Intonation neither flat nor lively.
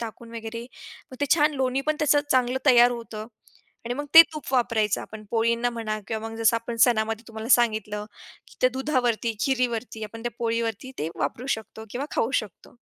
No: narrow, 2.3 semitones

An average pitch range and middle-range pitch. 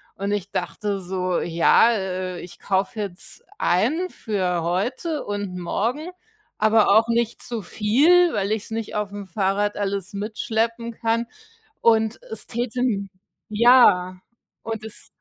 No: average, 3.2 semitones; high, 210 Hz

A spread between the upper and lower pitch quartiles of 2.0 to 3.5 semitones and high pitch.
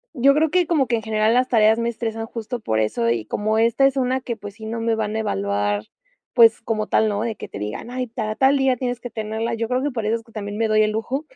Yes: narrow, 2.5 semitones; high, 225 Hz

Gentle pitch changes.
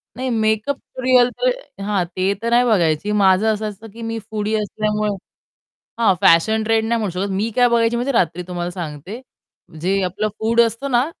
No: average, 3.3 semitones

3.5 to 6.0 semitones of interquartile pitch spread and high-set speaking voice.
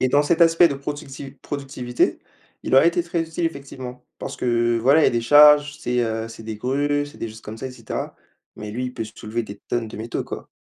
No: average, 3.8 semitones; low, 130 Hz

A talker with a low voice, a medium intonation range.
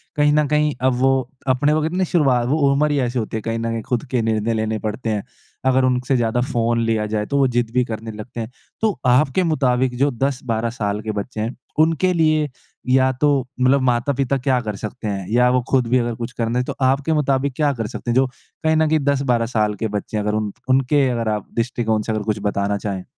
Yes: low, 125 Hz; average, 3.6 semitones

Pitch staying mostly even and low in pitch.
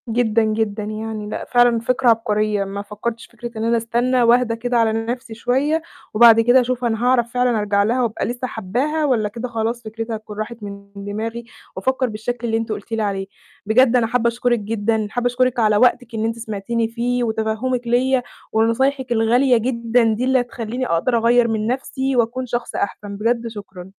No: narrow, 2.1 semitones; high, 230 Hz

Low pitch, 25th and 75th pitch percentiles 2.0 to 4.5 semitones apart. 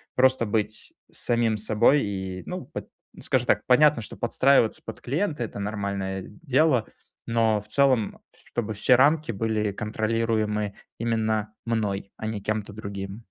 Yes: low, 110 Hz; narrow, 2.4 semitones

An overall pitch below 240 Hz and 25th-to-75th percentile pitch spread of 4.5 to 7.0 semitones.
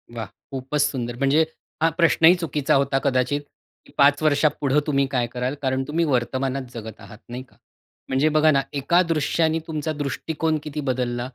No: medium, 140 Hz; average, 2.9 semitones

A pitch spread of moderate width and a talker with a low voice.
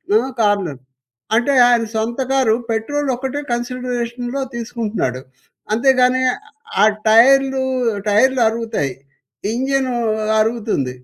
No: average, 3.0 semitones; high, 240 Hz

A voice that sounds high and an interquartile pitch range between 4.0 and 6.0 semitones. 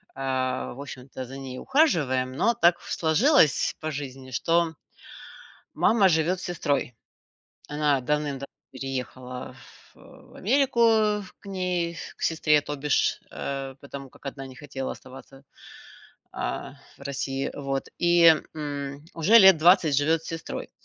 No: medium, 145 Hz; average, 4.3 semitones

